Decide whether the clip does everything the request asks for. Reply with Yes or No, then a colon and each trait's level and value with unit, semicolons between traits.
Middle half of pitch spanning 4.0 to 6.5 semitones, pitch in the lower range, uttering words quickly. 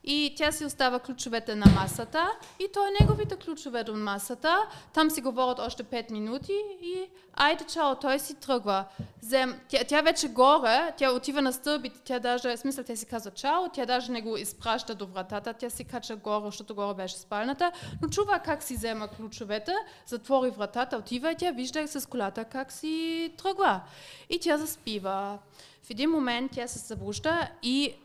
No: average, 5.2 semitones; very high, 255 Hz; fast, 180 wpm